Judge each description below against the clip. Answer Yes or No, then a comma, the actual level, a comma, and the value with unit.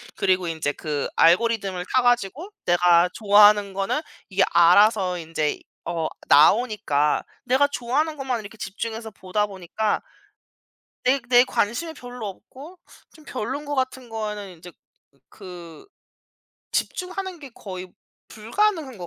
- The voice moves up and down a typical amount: No, wide, 6.0 semitones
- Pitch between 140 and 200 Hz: No, high, 210 Hz